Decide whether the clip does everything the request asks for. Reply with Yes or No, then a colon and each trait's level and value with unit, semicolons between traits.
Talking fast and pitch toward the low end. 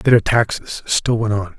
Yes: fast, 225 wpm; low, 110 Hz